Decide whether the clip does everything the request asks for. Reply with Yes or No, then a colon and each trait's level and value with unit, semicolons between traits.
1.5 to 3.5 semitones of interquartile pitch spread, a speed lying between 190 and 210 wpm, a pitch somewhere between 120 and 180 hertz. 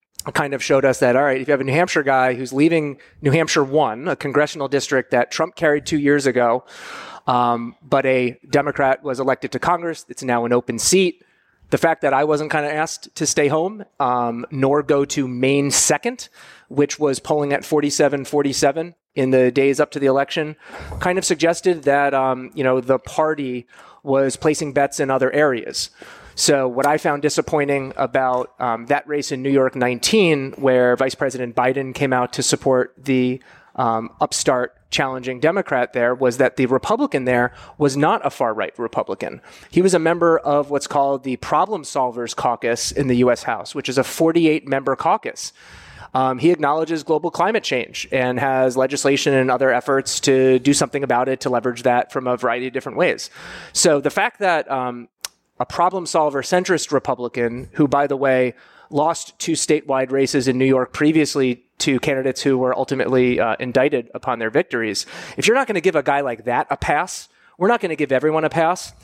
Yes: average, 2.9 semitones; average, 195 wpm; medium, 140 Hz